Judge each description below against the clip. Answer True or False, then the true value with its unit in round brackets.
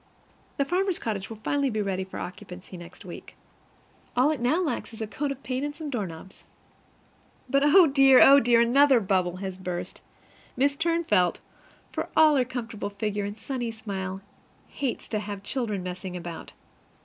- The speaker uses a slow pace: False (170 wpm)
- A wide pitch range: True (6.5 semitones)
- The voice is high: True (225 Hz)